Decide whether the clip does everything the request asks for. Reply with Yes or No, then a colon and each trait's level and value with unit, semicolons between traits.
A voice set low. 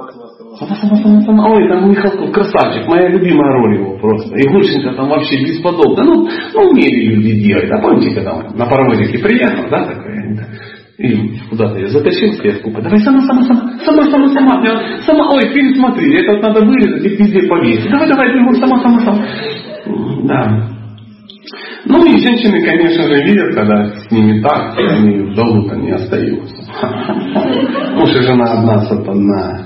No: medium, 175 Hz